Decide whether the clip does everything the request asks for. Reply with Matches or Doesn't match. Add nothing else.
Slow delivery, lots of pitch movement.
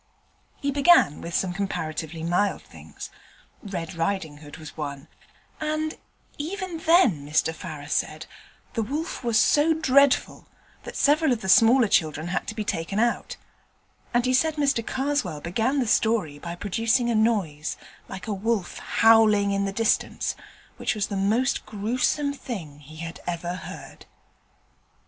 Doesn't match